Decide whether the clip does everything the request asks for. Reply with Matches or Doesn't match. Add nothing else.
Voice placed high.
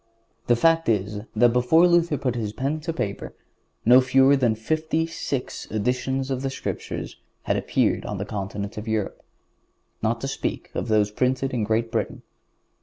Doesn't match